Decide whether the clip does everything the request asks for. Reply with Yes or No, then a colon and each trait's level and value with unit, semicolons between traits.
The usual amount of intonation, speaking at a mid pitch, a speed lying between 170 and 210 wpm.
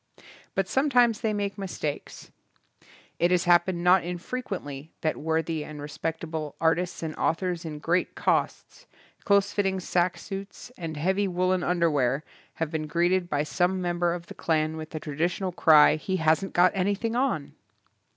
No: average, 3.1 semitones; medium, 175 Hz; average, 160 wpm